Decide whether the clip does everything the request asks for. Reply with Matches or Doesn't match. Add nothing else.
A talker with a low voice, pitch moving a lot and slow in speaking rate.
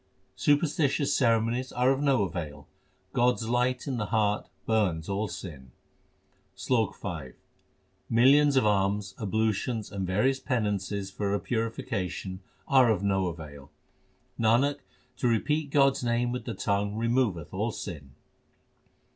Doesn't match